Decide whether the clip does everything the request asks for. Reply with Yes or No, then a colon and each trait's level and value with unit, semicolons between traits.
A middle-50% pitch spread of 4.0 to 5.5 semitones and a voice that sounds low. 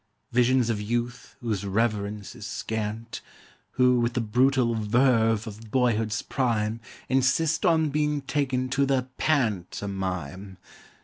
No: average, 3.5 semitones; low, 120 Hz